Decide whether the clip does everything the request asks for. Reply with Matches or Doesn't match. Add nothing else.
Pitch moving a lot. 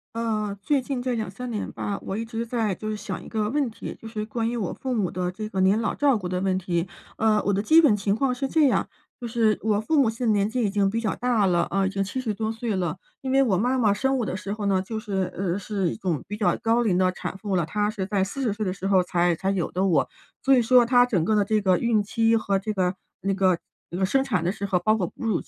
Doesn't match